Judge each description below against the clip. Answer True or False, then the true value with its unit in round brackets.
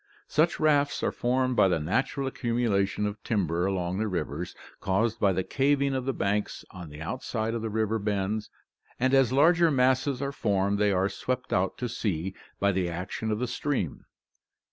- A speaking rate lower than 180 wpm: False (185 wpm)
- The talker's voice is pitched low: True (110 Hz)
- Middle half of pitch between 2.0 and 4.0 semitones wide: False (5.2 semitones)